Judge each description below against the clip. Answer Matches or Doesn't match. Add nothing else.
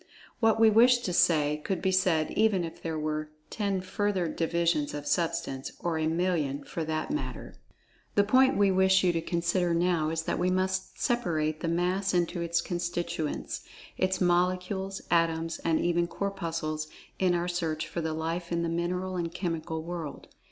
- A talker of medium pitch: Matches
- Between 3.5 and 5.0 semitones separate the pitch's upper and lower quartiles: Doesn't match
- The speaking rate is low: Doesn't match